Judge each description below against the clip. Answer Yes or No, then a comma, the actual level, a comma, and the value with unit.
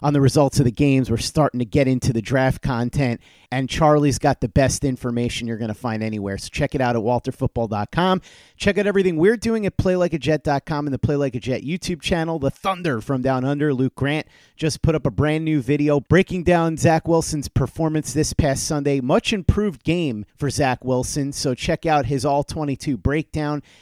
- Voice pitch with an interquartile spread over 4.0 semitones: No, average, 3.5 semitones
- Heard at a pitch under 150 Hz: Yes, medium, 140 Hz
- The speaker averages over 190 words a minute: Yes, fast, 205 wpm